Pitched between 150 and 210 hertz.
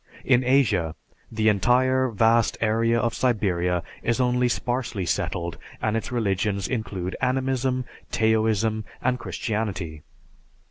No: low, 115 Hz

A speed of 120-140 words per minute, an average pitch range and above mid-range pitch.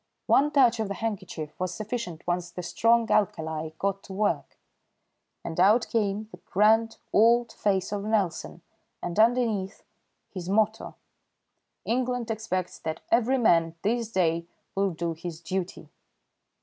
Yes: slow, 135 wpm; average, 4.4 semitones; high, 200 Hz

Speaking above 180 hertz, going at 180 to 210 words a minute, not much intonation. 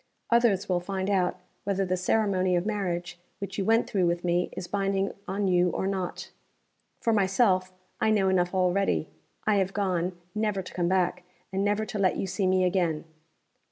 Yes: high, 190 Hz; average, 185 wpm; narrow, 1.9 semitones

